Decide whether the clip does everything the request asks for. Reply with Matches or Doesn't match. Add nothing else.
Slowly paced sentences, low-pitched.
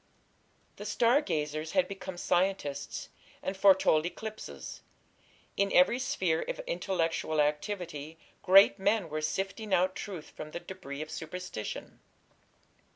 Doesn't match